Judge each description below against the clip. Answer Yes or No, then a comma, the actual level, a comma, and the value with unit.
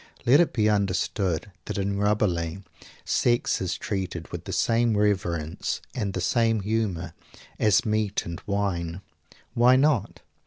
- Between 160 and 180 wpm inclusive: No, average, 140 wpm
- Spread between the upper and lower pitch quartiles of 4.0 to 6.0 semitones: No, average, 3.5 semitones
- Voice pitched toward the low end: Yes, low, 100 Hz